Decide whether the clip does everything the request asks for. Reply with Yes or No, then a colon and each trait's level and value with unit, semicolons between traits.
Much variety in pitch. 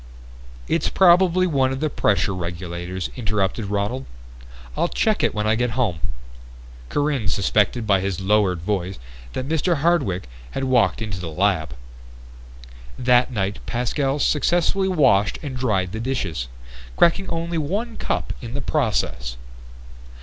Yes: wide, 7.1 semitones